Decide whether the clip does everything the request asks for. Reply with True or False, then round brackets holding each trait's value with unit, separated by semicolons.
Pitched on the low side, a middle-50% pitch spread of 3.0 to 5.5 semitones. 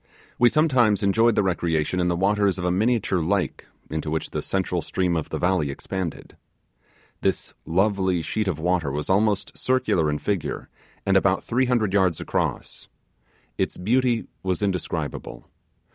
True (95 Hz; 3.6 semitones)